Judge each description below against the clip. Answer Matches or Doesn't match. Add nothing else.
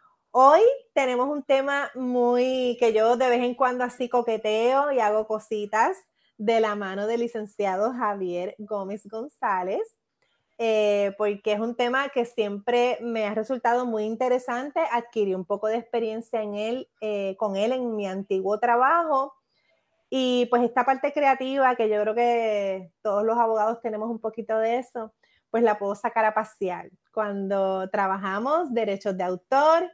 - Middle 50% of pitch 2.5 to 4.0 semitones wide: Matches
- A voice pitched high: Matches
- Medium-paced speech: Matches